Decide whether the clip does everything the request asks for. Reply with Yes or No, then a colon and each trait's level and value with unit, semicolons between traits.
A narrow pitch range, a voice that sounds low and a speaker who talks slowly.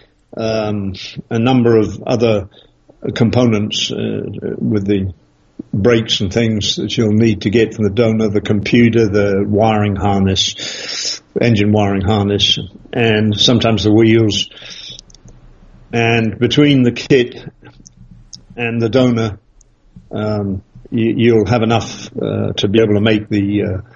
Yes: narrow, 2.1 semitones; low, 110 Hz; slow, 130 wpm